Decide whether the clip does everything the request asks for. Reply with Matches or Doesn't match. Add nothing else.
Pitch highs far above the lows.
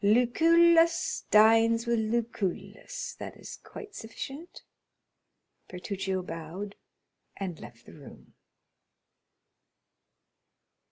Matches